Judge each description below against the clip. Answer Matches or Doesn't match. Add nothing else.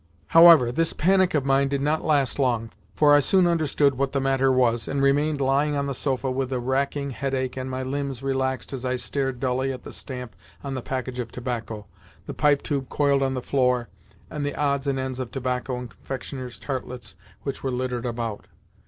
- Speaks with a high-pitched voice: Doesn't match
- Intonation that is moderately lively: Doesn't match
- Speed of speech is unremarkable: Doesn't match